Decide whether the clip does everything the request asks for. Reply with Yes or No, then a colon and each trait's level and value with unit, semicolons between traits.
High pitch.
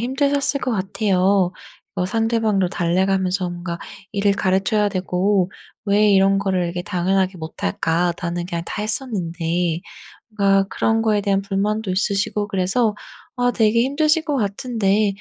Yes: high, 195 Hz